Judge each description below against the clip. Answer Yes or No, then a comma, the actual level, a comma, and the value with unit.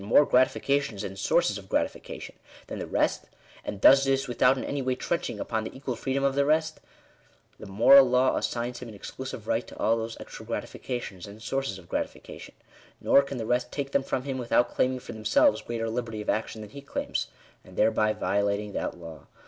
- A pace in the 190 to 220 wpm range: Yes, fast, 205 wpm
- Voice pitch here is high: No, low, 120 Hz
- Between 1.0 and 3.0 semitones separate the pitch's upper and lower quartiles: No, average, 4.0 semitones